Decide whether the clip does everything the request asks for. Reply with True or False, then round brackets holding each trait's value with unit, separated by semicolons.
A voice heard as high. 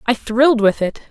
True (235 Hz)